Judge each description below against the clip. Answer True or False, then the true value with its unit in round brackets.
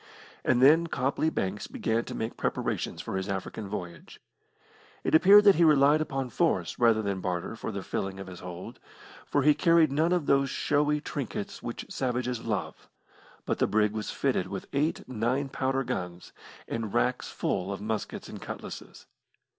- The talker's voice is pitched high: False (125 Hz)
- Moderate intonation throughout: False (7.0 semitones)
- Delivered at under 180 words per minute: True (170 wpm)